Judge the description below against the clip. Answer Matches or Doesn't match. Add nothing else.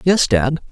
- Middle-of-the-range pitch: Matches